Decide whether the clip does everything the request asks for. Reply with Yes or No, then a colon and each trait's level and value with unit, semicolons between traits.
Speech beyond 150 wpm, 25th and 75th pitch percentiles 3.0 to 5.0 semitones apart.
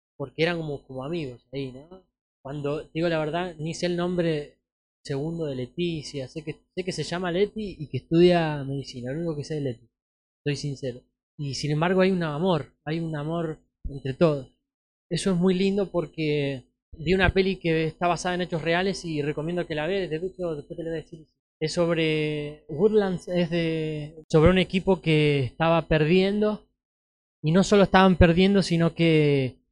Yes: average, 185 wpm; average, 3.5 semitones